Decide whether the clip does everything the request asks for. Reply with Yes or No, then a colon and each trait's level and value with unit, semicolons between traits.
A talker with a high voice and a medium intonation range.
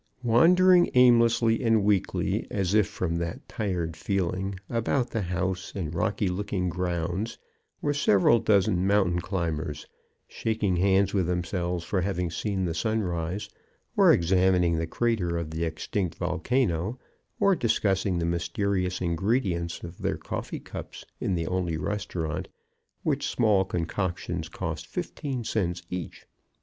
No: very low, 95 Hz; average, 3.5 semitones